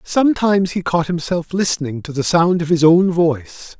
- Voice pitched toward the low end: No, medium, 170 Hz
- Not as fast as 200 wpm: Yes, average, 190 wpm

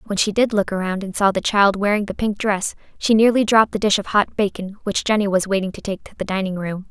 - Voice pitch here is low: No, high, 200 Hz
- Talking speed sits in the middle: No, fast, 270 wpm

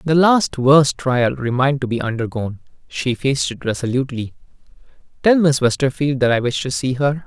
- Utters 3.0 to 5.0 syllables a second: No, 5.5 syllables/s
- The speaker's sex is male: Yes, male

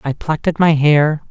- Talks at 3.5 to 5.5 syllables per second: Yes, 5.2 syllables/s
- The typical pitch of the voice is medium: Yes, medium, 150 Hz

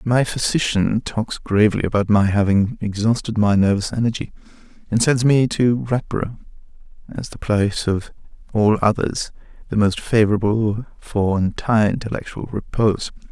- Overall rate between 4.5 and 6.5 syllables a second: Yes, 5.0 syllables/s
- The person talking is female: No, male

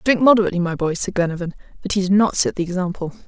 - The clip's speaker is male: No, female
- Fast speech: Yes, fast, 240 wpm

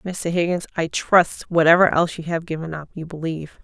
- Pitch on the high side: No, medium, 165 Hz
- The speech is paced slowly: No, average, 200 wpm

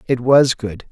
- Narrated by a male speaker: Yes, male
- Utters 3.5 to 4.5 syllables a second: Yes, 3.9 syllables/s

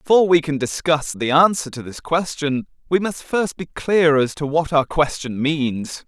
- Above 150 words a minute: Yes, average, 200 wpm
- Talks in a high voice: No, medium, 155 Hz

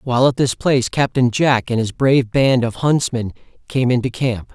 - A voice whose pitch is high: No, low, 125 Hz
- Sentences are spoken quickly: Yes, fast, 235 wpm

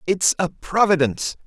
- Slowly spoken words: Yes, slow, 125 wpm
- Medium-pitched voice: Yes, medium, 170 Hz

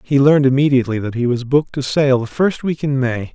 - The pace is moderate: No, fast, 250 wpm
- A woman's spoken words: No, male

